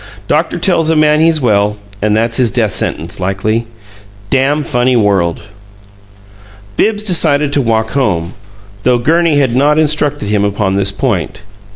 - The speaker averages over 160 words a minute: No, average, 150 wpm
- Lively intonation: Yes, wide, 6.5 semitones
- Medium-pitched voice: No, low, 120 Hz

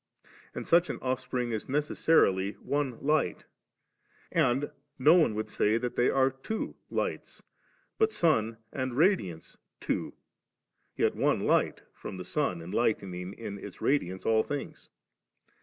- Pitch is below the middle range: Yes, low, 125 Hz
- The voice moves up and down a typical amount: No, wide, 5.9 semitones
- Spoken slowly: No, average, 145 wpm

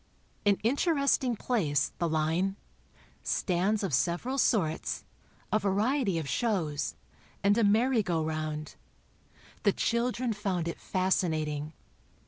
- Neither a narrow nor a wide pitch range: No, wide, 6.3 semitones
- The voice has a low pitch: No, high, 195 Hz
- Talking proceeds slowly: Yes, slow, 110 wpm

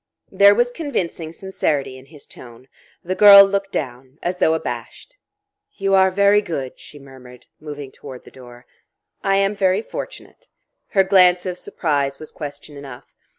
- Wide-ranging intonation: Yes, wide, 6.2 semitones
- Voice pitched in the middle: Yes, medium, 165 Hz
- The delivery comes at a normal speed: Yes, average, 155 wpm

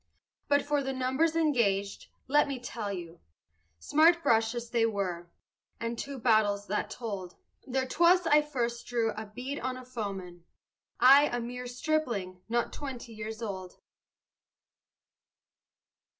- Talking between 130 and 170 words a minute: Yes, slow, 135 wpm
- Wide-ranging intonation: No, average, 4.6 semitones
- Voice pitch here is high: Yes, high, 235 Hz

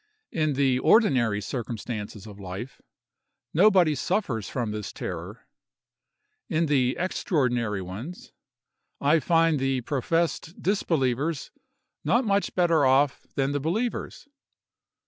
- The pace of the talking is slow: Yes, slow, 105 wpm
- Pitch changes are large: Yes, wide, 5.7 semitones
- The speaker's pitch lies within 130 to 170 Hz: Yes, medium, 140 Hz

